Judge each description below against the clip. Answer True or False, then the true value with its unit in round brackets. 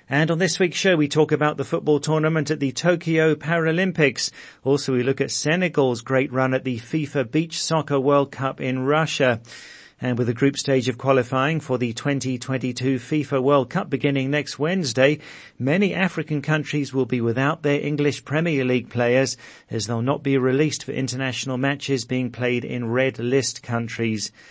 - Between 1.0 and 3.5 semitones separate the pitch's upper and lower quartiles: True (2.8 semitones)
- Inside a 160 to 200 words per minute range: True (175 wpm)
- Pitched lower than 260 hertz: True (135 Hz)